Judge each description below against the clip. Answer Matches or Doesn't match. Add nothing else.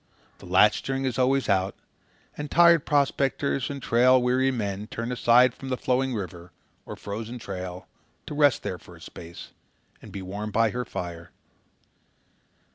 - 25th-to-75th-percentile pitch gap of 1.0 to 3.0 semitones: Doesn't match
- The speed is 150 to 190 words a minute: Matches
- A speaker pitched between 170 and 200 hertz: Doesn't match